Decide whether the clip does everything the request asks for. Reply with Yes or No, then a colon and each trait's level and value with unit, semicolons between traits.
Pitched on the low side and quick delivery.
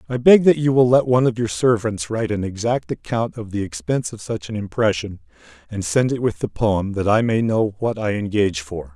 Yes: low, 115 Hz; fast, 235 wpm